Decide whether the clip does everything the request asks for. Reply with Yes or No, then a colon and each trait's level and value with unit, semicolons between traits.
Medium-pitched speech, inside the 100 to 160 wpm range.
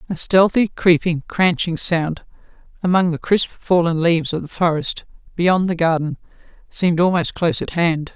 Yes: medium, 170 Hz; average, 155 wpm